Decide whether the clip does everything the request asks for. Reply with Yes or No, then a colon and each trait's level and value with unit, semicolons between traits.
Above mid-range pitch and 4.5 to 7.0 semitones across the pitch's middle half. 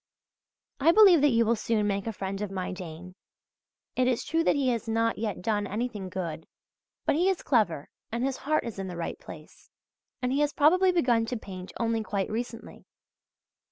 Yes: high, 225 Hz; average, 5.3 semitones